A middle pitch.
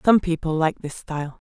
Yes: medium, 160 Hz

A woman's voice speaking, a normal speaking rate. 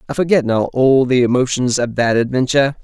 No: male; average, 190 wpm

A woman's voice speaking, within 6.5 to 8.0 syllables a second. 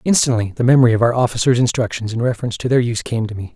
No: male; 7.9 syllables/s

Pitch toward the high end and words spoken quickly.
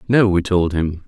No: very low, 95 Hz; fast, 225 wpm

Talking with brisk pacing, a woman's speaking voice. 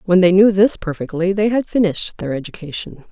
No: average, 195 wpm; female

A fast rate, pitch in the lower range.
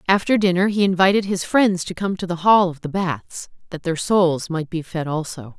No: fast, 225 wpm; medium, 180 Hz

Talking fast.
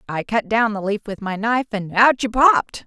Yes: fast, 230 wpm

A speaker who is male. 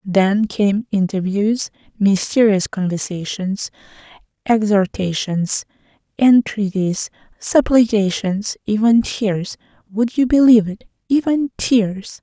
No: female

